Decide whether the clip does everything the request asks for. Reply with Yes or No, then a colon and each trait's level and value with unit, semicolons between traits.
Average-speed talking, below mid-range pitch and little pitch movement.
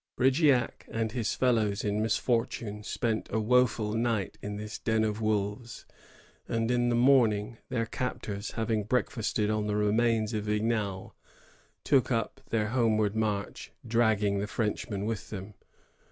Yes: average, 145 wpm; low, 110 Hz; narrow, 2.0 semitones